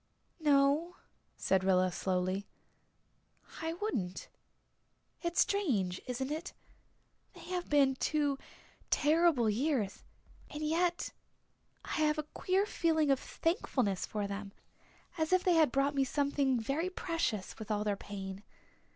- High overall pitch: Yes, very high, 280 Hz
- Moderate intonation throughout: No, wide, 7.8 semitones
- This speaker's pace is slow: Yes, slow, 125 wpm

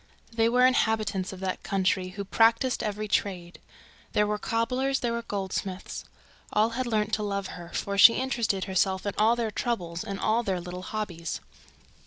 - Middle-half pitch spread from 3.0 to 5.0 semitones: Yes, average, 3.3 semitones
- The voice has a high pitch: Yes, high, 210 Hz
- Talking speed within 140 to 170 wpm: No, average, 200 wpm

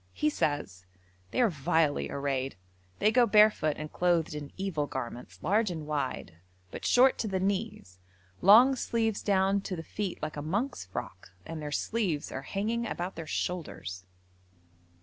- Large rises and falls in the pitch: Yes, wide, 6.3 semitones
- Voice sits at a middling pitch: Yes, medium, 170 Hz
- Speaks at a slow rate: No, average, 160 wpm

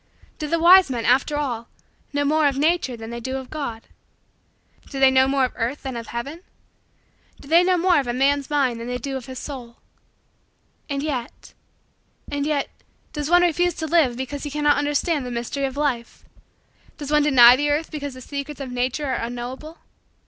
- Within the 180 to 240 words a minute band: Yes, average, 200 wpm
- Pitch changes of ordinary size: Yes, average, 3.1 semitones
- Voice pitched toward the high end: Yes, very high, 275 Hz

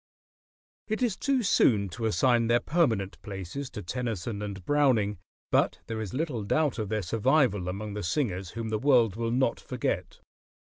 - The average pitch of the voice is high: No, low, 115 Hz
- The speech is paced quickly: No, average, 175 wpm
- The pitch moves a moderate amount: Yes, average, 4.6 semitones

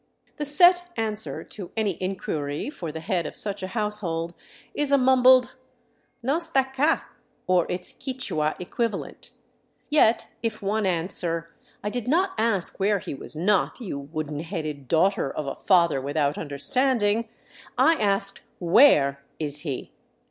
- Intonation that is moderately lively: No, wide, 7.3 semitones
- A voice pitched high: Yes, high, 195 Hz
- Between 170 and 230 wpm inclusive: No, average, 150 wpm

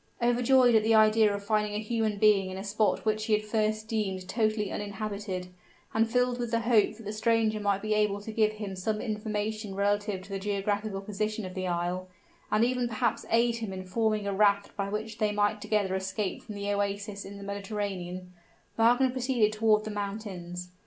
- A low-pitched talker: No, high, 210 Hz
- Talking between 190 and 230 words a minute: Yes, average, 200 wpm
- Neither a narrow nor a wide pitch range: No, narrow, 1.6 semitones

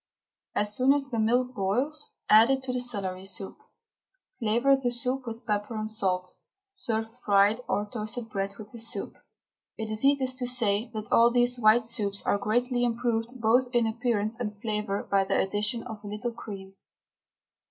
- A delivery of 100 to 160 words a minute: No, average, 175 wpm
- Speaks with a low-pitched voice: No, high, 225 Hz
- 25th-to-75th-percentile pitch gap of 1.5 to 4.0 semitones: Yes, average, 2.9 semitones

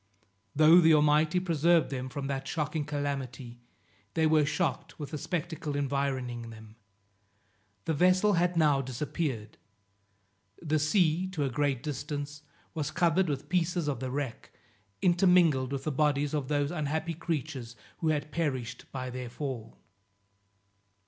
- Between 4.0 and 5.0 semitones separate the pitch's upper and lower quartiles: No, average, 3.2 semitones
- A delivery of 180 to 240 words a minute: No, average, 140 wpm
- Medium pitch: Yes, medium, 150 Hz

